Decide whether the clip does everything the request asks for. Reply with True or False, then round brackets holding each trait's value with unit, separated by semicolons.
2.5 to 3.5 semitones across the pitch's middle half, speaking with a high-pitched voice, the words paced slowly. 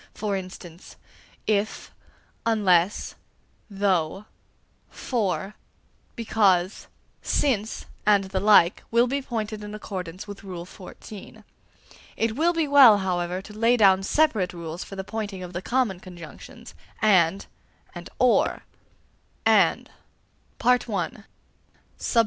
True (3.2 semitones; 200 Hz; 110 wpm)